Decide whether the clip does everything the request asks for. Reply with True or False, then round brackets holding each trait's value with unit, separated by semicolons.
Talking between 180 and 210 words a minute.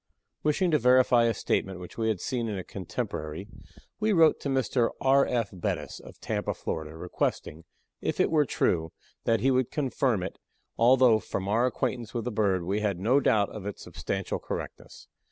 True (185 wpm)